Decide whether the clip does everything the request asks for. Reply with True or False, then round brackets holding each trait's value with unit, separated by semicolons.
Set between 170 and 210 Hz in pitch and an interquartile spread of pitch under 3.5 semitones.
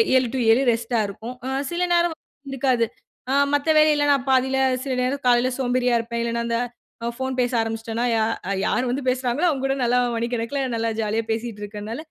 False (245 Hz; 2.6 semitones)